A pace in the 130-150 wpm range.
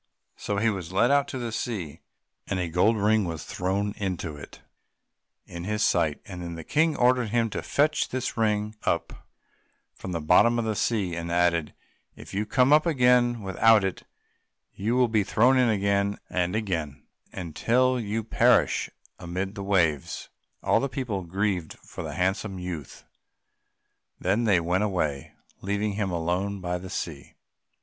No: average, 165 wpm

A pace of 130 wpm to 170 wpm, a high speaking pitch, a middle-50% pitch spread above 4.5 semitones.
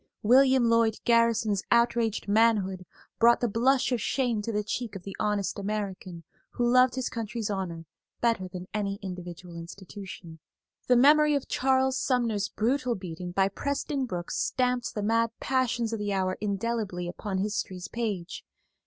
No: average, 155 wpm; high, 215 Hz; average, 3.9 semitones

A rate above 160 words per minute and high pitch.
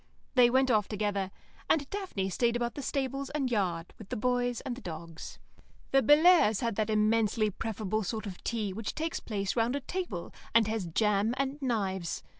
Yes: average, 185 wpm; high, 225 Hz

